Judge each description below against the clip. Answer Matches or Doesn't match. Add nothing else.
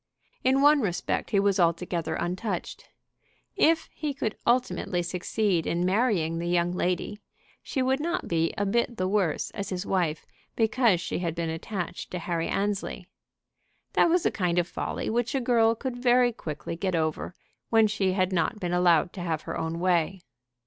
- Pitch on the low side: Doesn't match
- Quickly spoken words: Doesn't match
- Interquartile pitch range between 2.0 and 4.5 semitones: Doesn't match